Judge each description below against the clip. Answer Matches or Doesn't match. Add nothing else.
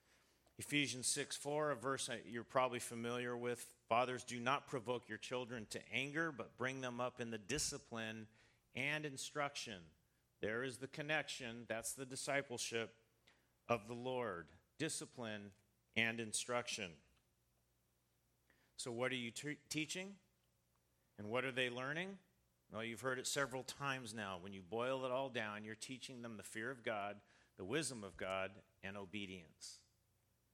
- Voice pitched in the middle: Doesn't match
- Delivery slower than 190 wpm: Matches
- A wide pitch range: Doesn't match